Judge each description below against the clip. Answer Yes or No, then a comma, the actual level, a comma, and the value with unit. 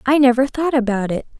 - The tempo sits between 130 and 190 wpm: No, fast, 215 wpm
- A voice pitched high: Yes, very high, 255 Hz